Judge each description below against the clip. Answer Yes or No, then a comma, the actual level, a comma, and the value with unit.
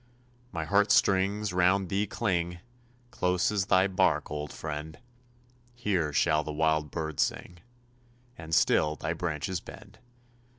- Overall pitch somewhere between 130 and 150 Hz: No, very low, 90 Hz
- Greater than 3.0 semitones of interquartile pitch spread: Yes, average, 3.7 semitones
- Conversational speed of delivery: No, slow, 130 wpm